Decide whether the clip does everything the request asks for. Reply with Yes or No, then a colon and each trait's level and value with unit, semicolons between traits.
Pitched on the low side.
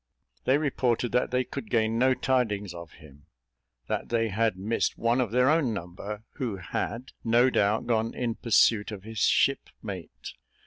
Yes: low, 115 Hz